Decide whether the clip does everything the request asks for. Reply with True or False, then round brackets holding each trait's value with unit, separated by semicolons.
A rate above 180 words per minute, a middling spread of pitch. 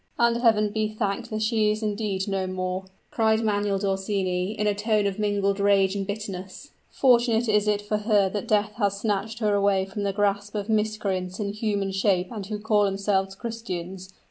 False (190 wpm; 1.8 semitones)